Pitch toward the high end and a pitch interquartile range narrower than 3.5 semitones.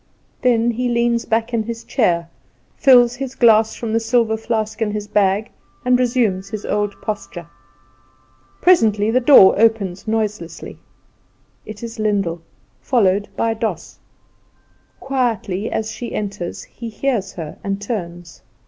Yes: high, 220 Hz; average, 2.7 semitones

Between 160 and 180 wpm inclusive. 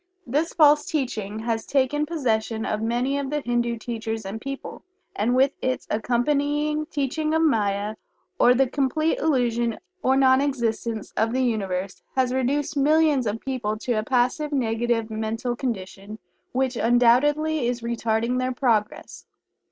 No: average, 145 wpm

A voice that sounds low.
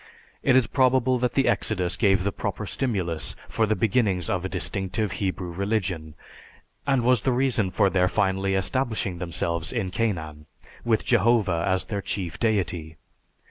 Yes: low, 100 Hz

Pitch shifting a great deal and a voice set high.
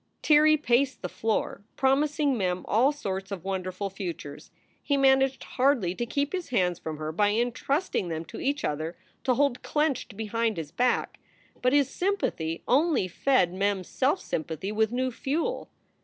Yes: wide, 7.0 semitones; high, 235 Hz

